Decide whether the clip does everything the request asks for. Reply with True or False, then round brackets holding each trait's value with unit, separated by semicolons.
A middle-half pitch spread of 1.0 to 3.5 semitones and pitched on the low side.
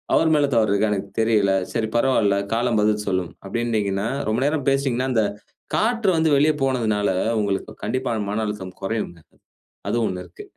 False (4.3 semitones; 110 Hz)